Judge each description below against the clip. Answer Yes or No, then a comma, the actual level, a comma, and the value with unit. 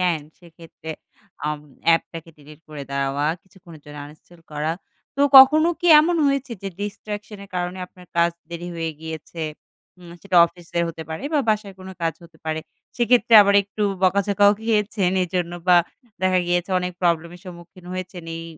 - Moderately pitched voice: Yes, medium, 175 Hz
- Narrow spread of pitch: No, average, 3.5 semitones